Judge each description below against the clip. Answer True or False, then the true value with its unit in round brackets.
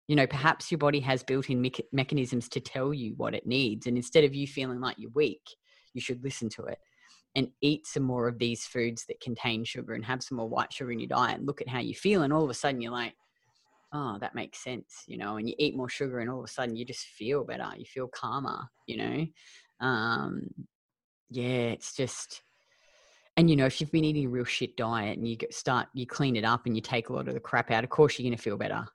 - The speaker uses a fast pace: True (255 wpm)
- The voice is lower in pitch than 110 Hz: False (125 Hz)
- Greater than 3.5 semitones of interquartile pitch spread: False (2.9 semitones)